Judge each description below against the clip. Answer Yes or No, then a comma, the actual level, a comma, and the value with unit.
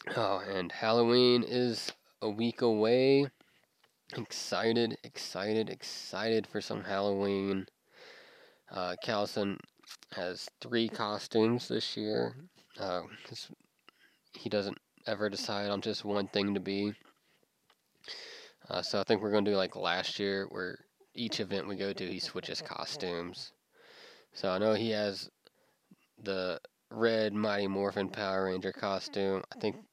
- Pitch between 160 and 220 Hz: No, low, 105 Hz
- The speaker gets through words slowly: Yes, slow, 130 wpm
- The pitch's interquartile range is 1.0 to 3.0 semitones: Yes, narrow, 2.5 semitones